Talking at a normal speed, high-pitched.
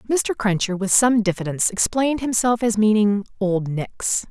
Yes: average, 155 wpm; high, 215 Hz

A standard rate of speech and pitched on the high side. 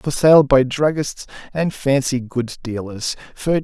No: average, 150 wpm; low, 135 Hz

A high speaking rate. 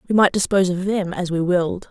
Yes: fast, 250 wpm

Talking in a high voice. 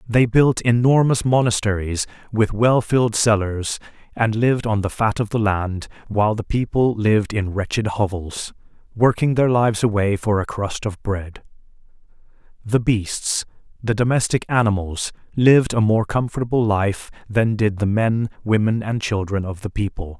No: low, 110 Hz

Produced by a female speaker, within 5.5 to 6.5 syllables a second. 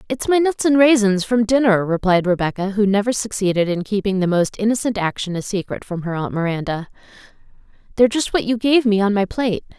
Yes: female; 6.0 syllables/s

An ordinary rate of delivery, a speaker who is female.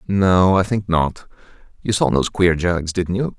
No: average, 195 wpm; male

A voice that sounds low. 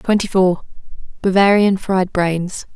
No: high, 190 Hz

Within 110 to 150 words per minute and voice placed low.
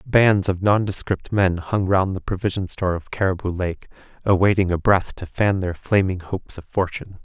No: average, 180 wpm; very low, 95 Hz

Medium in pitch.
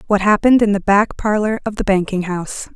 No: high, 205 Hz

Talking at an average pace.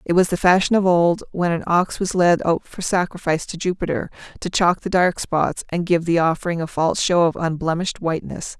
No: fast, 215 wpm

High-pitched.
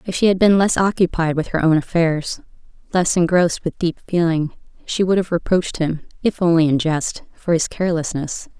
No: medium, 170 Hz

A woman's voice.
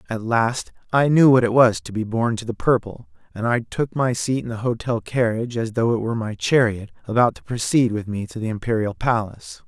No: male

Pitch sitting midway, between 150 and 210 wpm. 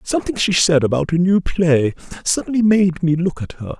Yes: medium, 175 Hz; average, 175 wpm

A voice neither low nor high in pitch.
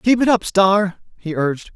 No: high, 195 Hz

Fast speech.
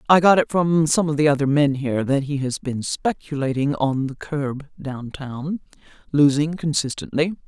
No: average, 170 wpm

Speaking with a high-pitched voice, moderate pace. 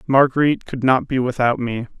No: low, 130 Hz; average, 180 wpm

